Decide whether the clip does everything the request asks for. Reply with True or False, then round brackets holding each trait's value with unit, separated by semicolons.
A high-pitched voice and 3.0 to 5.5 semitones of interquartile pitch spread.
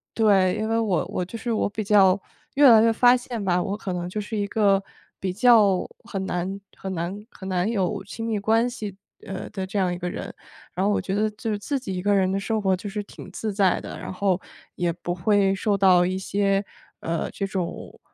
False (195 Hz; 2.6 semitones)